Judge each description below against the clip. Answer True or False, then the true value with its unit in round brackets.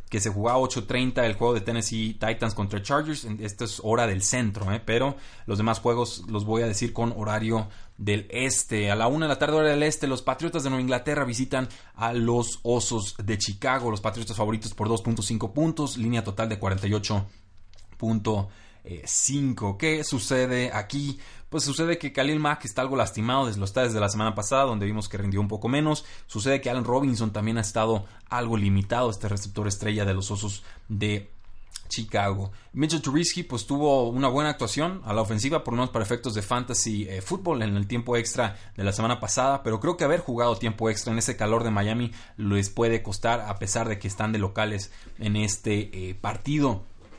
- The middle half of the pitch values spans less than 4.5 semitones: True (3.5 semitones)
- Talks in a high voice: False (115 Hz)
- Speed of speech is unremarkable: False (200 wpm)